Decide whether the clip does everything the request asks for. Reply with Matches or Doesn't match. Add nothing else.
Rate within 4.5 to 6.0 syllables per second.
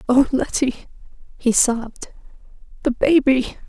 Doesn't match